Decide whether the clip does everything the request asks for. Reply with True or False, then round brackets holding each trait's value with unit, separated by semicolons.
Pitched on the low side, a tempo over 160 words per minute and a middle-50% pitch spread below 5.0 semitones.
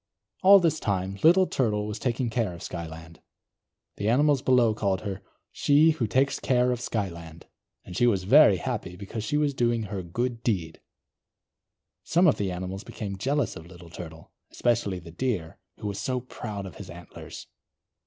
False (105 Hz; 175 wpm; 5.6 semitones)